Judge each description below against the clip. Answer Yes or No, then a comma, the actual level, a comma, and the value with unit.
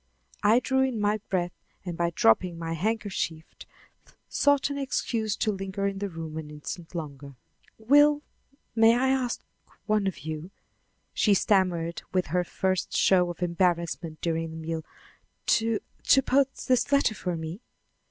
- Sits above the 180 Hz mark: Yes, high, 190 Hz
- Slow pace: No, average, 150 wpm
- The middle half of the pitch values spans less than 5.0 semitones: No, average, 5.3 semitones